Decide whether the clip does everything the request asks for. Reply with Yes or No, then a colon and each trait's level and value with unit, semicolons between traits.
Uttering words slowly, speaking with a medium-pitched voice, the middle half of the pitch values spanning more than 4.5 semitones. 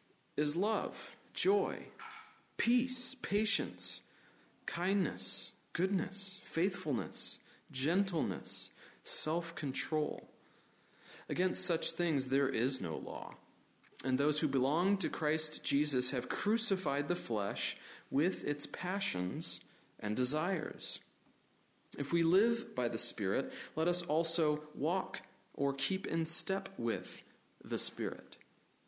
Yes: slow, 105 wpm; medium, 170 Hz; average, 5.3 semitones